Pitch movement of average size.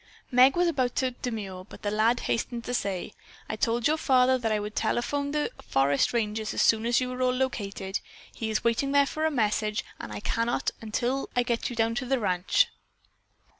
Yes: average, 3.2 semitones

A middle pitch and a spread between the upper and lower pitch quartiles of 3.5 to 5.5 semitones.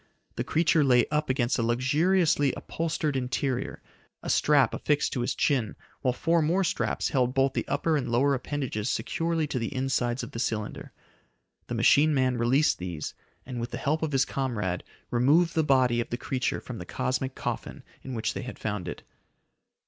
No: low, 130 Hz; average, 3.8 semitones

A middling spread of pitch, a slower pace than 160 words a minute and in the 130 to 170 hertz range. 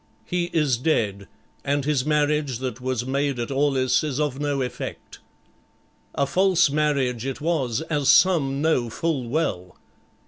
Yes: average, 3.1 semitones; average, 145 wpm; medium, 140 Hz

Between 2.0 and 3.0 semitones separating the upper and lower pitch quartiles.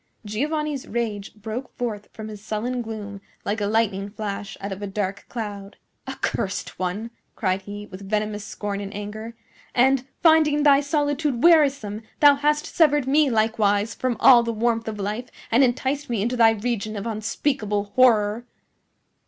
No: average, 4.0 semitones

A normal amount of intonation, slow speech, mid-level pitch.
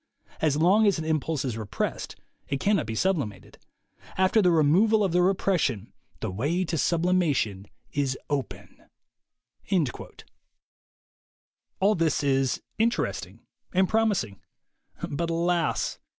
No: wide, 6.0 semitones; slow, 115 wpm; medium, 160 Hz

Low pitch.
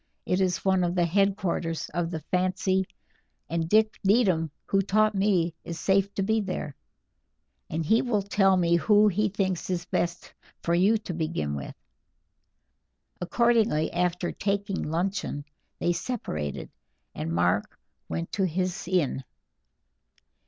No: medium, 185 Hz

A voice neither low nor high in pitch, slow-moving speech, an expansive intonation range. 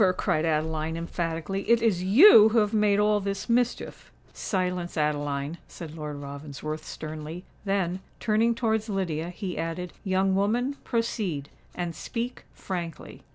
No: medium, 180 Hz; slow, 130 wpm; average, 5.0 semitones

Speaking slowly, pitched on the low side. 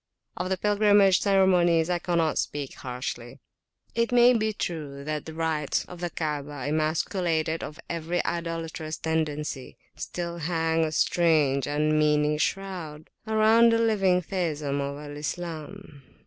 No: slow, 130 wpm; medium, 165 Hz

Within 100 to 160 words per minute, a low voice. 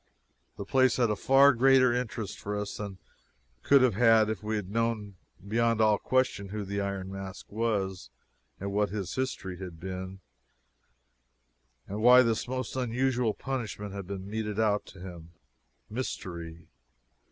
Yes: average, 155 wpm; low, 105 Hz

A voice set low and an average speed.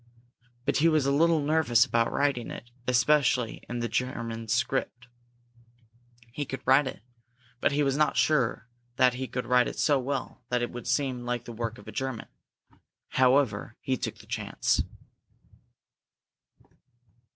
Yes: low, 125 Hz; average, 155 wpm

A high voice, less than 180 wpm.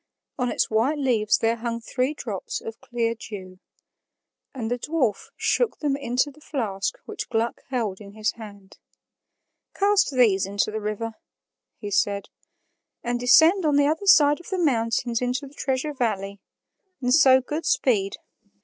Yes: high, 240 Hz; average, 160 wpm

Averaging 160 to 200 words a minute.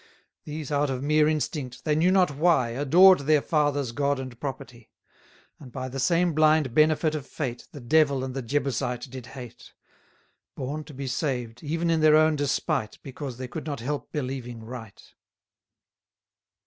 Yes: average, 165 wpm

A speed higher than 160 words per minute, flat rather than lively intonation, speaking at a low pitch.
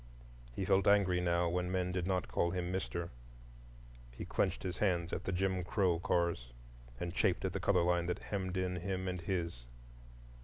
Yes: average, 185 wpm; narrow, 1.5 semitones; very low, 90 Hz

